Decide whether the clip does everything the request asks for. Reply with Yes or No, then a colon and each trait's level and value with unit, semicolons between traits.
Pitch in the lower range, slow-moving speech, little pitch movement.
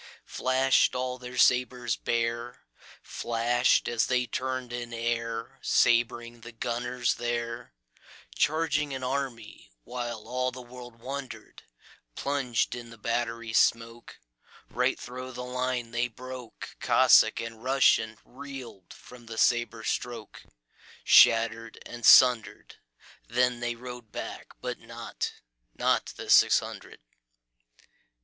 Yes: low, 120 Hz; slow, 95 wpm; narrow, 1.6 semitones